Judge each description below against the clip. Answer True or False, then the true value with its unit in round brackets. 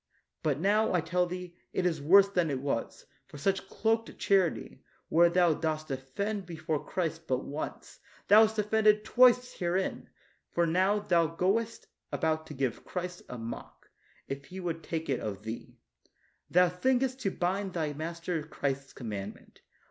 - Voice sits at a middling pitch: True (175 Hz)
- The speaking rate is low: False (165 wpm)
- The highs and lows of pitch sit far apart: False (4.3 semitones)